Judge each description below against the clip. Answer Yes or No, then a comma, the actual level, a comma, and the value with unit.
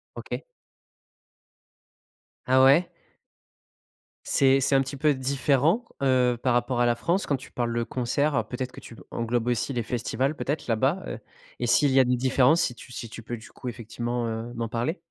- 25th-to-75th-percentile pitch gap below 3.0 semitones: Yes, narrow, 2.5 semitones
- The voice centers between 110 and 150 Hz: Yes, low, 125 Hz